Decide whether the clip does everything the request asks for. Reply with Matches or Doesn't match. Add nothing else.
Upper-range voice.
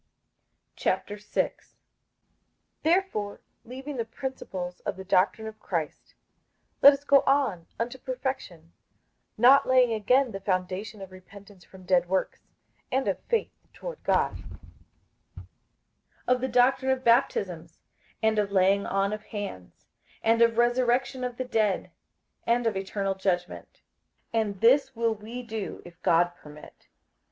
Matches